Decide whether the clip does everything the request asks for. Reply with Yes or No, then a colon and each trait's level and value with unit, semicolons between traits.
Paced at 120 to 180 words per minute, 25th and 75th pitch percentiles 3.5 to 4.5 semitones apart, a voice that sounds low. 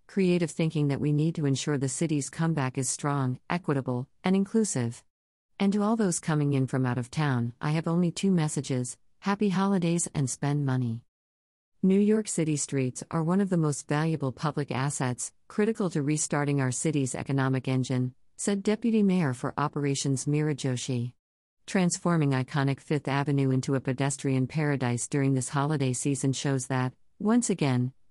No: average, 165 wpm; average, 4.2 semitones; medium, 145 Hz